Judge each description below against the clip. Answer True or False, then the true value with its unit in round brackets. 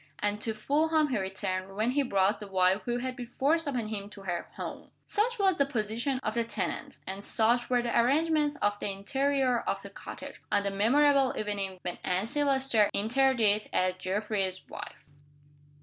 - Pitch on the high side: True (225 Hz)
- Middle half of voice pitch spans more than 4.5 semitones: True (5.3 semitones)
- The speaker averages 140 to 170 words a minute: False (185 wpm)